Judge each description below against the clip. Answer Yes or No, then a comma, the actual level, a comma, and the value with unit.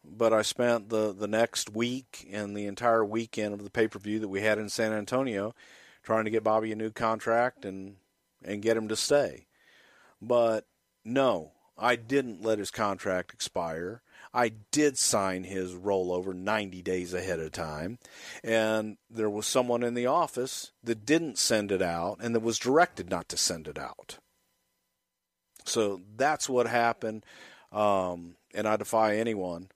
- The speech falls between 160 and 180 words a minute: Yes, average, 165 wpm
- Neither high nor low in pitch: No, low, 110 Hz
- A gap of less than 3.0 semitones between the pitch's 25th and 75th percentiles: Yes, narrow, 2.5 semitones